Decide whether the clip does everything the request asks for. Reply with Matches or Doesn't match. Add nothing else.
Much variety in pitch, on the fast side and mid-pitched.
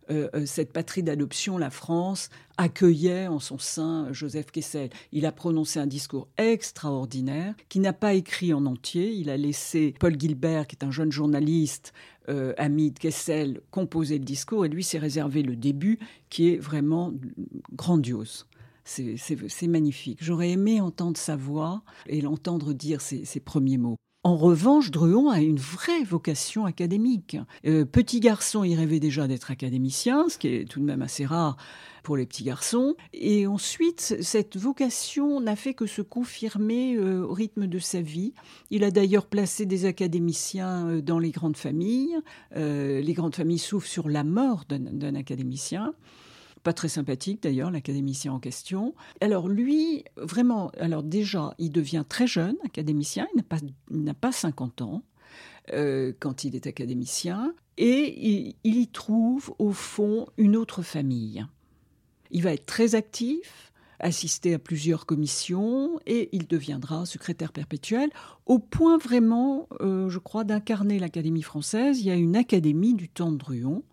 Doesn't match